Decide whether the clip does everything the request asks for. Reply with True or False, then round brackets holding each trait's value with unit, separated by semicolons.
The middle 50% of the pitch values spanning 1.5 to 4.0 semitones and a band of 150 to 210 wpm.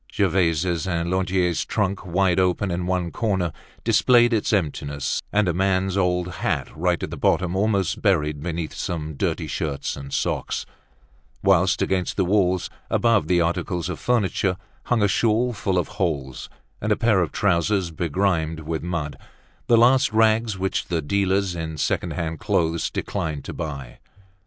True (3.3 semitones; 160 wpm)